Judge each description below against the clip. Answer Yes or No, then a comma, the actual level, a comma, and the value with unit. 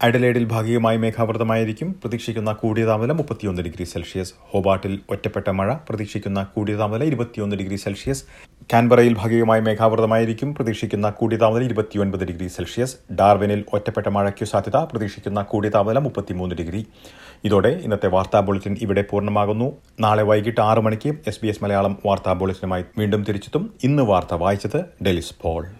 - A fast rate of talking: Yes, fast, 135 wpm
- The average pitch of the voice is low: Yes, low, 105 Hz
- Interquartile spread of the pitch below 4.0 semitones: Yes, narrow, 2.6 semitones